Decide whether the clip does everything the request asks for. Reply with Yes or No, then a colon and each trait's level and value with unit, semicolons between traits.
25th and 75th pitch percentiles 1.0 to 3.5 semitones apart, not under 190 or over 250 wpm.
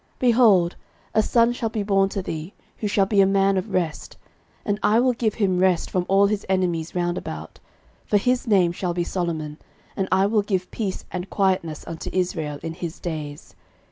Yes: average, 3.0 semitones; average, 200 wpm